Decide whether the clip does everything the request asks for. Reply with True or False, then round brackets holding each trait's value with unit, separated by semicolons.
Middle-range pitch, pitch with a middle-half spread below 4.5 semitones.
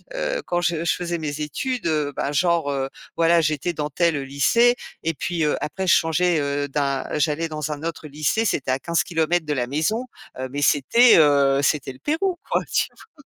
True (155 Hz; 3.5 semitones)